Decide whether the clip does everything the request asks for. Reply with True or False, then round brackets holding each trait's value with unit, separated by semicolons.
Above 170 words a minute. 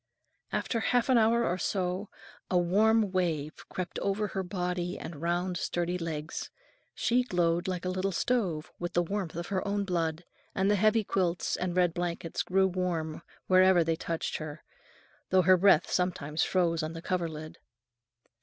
False (165 wpm)